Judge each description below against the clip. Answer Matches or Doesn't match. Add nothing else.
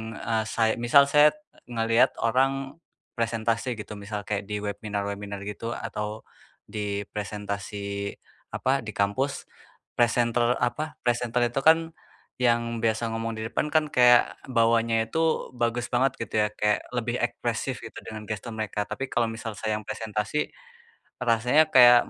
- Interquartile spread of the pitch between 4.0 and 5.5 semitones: Doesn't match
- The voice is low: Matches